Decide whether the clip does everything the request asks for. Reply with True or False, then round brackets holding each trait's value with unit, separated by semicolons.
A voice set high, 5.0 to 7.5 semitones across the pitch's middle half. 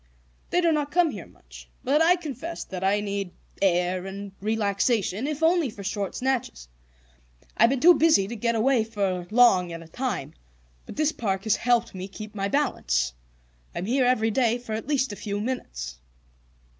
True (220 Hz; 5.5 semitones)